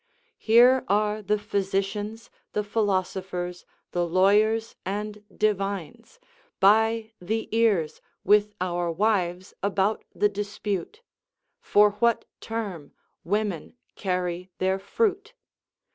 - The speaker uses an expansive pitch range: No, average, 2.8 semitones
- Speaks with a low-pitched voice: No, high, 205 Hz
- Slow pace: Yes, slow, 100 wpm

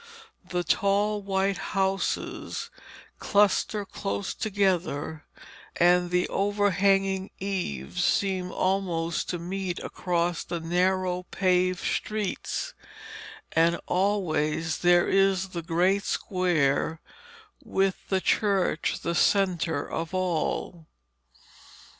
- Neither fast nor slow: No, slow, 95 wpm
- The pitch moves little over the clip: Yes, narrow, 2.2 semitones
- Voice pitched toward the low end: No, medium, 185 Hz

